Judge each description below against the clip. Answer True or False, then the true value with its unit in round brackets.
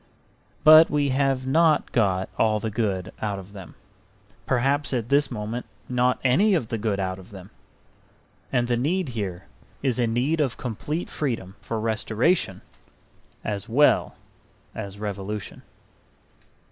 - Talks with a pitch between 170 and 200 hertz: False (115 Hz)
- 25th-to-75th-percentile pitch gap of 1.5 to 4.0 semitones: False (5.1 semitones)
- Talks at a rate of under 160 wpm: True (140 wpm)